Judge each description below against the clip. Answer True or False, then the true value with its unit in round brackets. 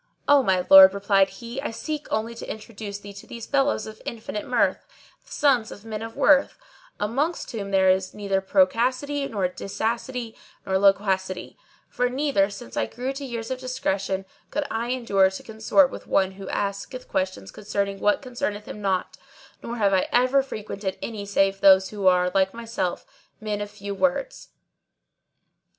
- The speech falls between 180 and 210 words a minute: False (170 wpm)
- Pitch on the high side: True (210 Hz)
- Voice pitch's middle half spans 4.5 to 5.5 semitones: False (4.0 semitones)